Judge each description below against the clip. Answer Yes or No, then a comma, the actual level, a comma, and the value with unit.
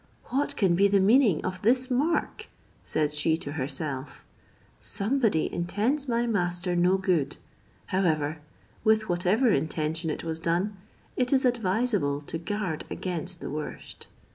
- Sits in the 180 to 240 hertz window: Yes, medium, 185 Hz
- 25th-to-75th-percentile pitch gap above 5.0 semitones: Yes, wide, 5.6 semitones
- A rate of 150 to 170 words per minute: No, average, 140 wpm